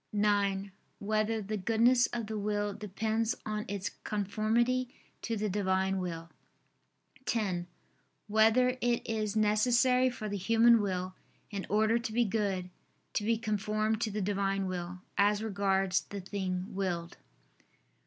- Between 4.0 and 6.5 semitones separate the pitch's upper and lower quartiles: No, narrow, 2.4 semitones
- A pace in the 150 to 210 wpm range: No, slow, 135 wpm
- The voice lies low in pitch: No, high, 210 Hz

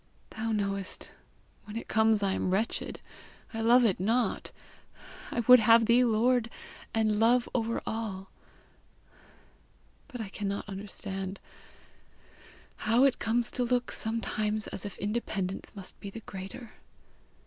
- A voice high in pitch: Yes, high, 220 Hz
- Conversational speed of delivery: No, slow, 130 wpm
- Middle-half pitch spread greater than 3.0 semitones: No, average, 2.7 semitones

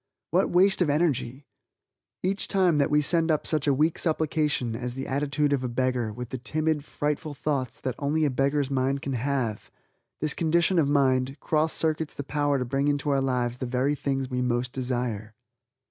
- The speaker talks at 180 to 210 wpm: Yes, average, 190 wpm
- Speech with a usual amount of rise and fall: Yes, average, 3.0 semitones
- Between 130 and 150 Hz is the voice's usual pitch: Yes, medium, 140 Hz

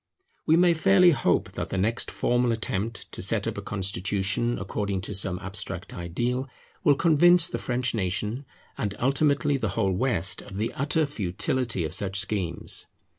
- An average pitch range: No, wide, 6.1 semitones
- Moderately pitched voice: No, low, 115 Hz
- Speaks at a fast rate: No, average, 165 wpm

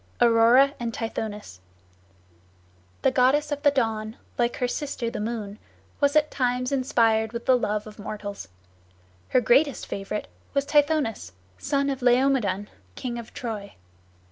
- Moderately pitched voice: No, high, 240 Hz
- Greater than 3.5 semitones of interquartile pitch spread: Yes, average, 3.9 semitones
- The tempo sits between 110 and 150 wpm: Yes, average, 140 wpm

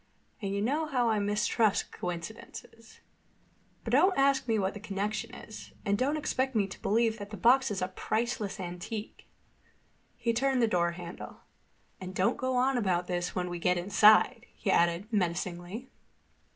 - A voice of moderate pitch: No, high, 210 Hz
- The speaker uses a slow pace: No, average, 165 wpm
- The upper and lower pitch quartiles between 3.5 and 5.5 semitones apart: Yes, average, 4.6 semitones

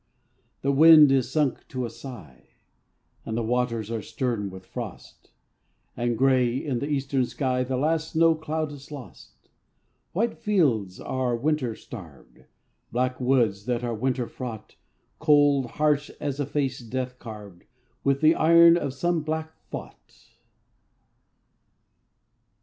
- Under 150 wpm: Yes, average, 140 wpm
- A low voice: Yes, low, 130 Hz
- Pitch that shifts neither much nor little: Yes, average, 4.1 semitones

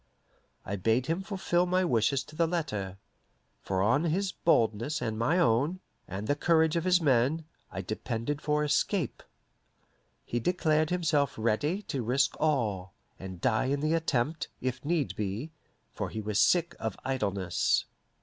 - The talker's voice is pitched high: No, medium, 140 Hz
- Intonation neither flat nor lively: No, wide, 6.6 semitones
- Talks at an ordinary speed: Yes, average, 155 wpm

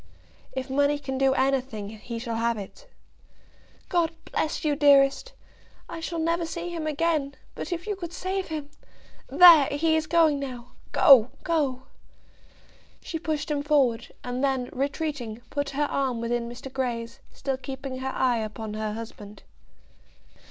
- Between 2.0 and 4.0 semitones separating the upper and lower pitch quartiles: No, average, 4.4 semitones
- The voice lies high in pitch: Yes, very high, 275 Hz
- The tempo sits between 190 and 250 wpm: No, average, 150 wpm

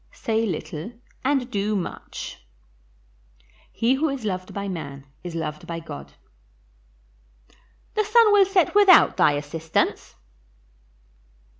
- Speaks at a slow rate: Yes, slow, 115 wpm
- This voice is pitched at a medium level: No, high, 200 Hz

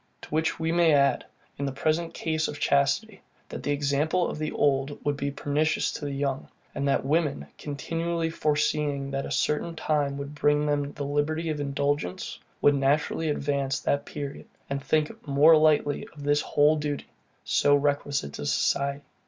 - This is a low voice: No, medium, 145 Hz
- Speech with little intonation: Yes, narrow, 1.7 semitones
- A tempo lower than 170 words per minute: No, average, 175 wpm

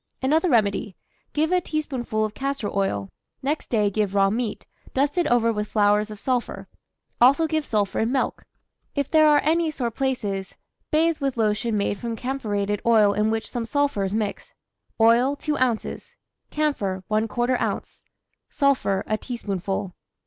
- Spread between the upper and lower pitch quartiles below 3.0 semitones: No, average, 5.1 semitones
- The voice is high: Yes, high, 230 Hz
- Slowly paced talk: No, average, 155 wpm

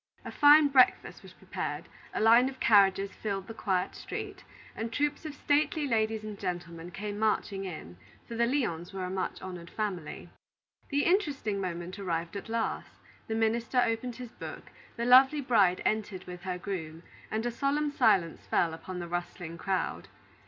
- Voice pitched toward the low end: No, high, 210 Hz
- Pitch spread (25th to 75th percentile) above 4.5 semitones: Yes, average, 5.3 semitones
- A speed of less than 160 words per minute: No, average, 170 wpm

